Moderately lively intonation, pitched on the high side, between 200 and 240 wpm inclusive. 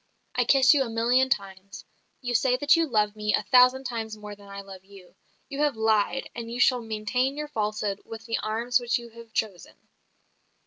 Yes: average, 3.2 semitones; high, 230 Hz; fast, 205 wpm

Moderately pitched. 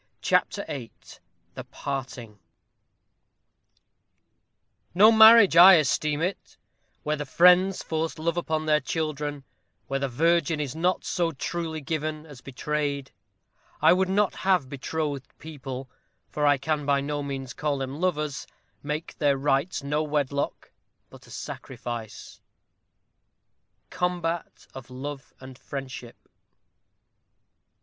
Yes: medium, 150 Hz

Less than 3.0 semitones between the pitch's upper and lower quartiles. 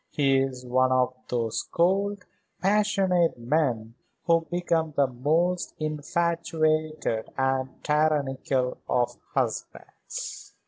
No: average, 4.7 semitones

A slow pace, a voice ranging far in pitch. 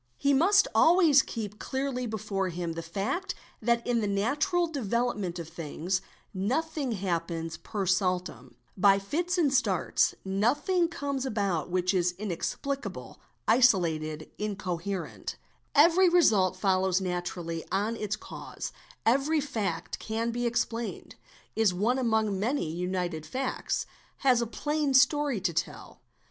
Yes: slow, 130 wpm; wide, 6.8 semitones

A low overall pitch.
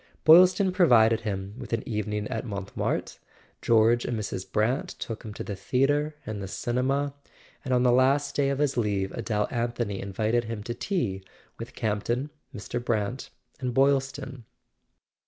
Yes: low, 120 Hz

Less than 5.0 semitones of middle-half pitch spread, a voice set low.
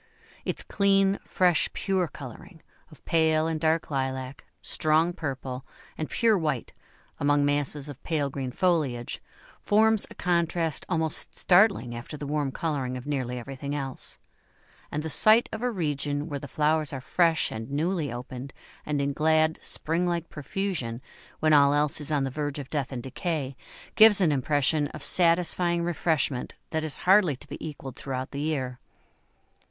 No: average, 3.6 semitones; medium, 150 Hz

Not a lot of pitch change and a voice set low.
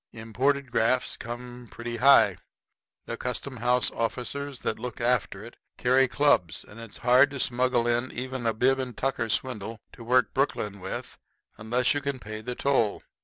Yes: narrow, 2.1 semitones; low, 125 Hz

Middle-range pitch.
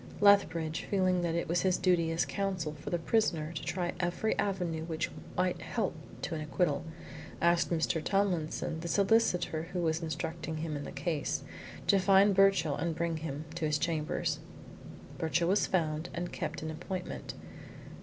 Yes: medium, 170 Hz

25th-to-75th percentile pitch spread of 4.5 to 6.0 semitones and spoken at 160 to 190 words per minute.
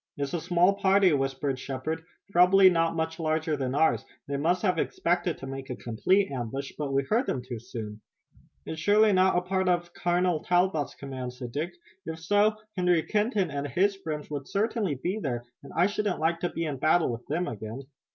No: average, 5.0 semitones; average, 200 wpm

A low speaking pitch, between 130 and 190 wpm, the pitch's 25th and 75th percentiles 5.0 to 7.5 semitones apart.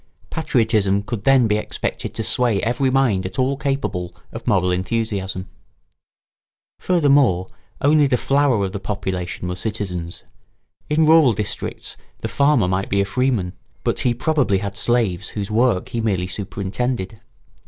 Yes: low, 110 Hz; average, 145 wpm; wide, 5.4 semitones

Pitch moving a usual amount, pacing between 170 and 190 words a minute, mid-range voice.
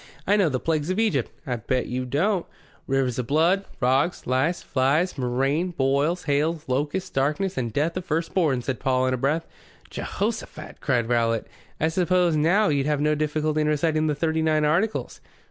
Yes: average, 3.9 semitones; average, 180 wpm; medium, 150 Hz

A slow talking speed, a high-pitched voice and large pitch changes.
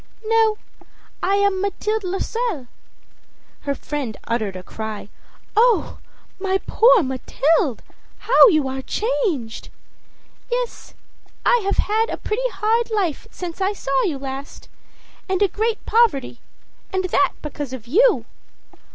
Yes: slow, 125 wpm; very high, 380 Hz; wide, 8.2 semitones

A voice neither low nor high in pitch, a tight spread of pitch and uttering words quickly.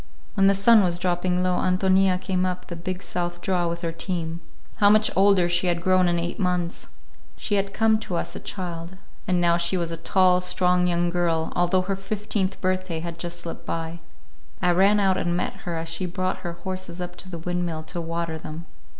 Yes: medium, 180 Hz; narrow, 1.6 semitones; fast, 210 wpm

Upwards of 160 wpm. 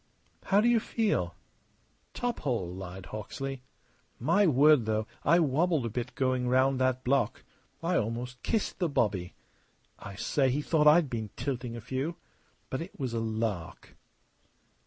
No: average, 155 wpm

